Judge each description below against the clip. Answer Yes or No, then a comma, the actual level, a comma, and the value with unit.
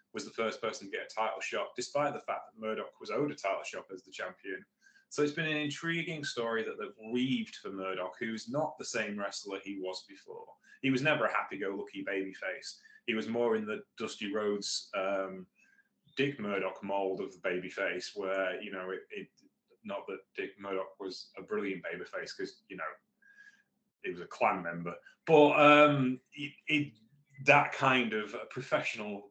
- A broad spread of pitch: Yes, wide, 6.9 semitones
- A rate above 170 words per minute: Yes, average, 190 wpm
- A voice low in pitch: Yes, low, 120 Hz